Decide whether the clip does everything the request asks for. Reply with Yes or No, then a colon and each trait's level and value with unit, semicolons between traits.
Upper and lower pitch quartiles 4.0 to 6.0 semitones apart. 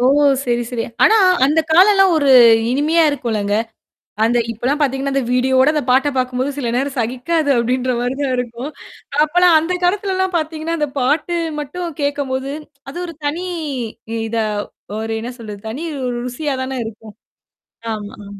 Yes: average, 4.3 semitones